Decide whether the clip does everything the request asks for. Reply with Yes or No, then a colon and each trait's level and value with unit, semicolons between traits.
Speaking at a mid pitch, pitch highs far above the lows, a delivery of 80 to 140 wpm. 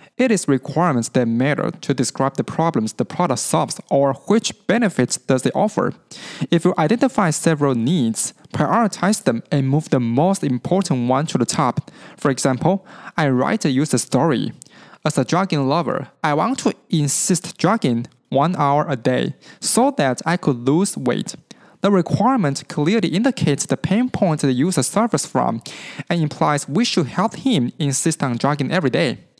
No: medium, 160 Hz; wide, 6.0 semitones; average, 165 wpm